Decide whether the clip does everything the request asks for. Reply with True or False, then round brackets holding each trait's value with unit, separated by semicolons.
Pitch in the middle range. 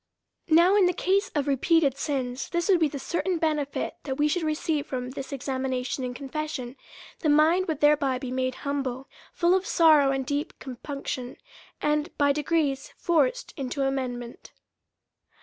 False (285 Hz)